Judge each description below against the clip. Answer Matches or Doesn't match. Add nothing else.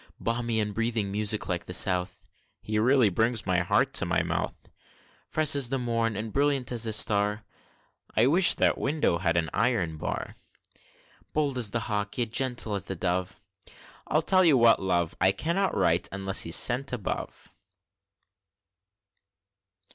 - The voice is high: Doesn't match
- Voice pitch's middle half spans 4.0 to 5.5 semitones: Matches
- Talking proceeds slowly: Doesn't match